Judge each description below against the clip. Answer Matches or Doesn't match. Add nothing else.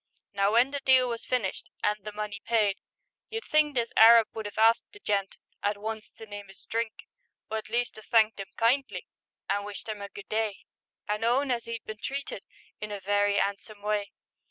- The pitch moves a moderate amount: Doesn't match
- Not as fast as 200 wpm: Doesn't match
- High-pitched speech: Matches